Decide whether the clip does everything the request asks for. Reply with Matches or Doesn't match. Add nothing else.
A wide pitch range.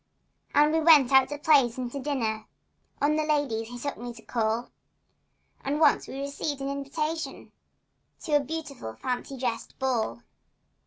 Doesn't match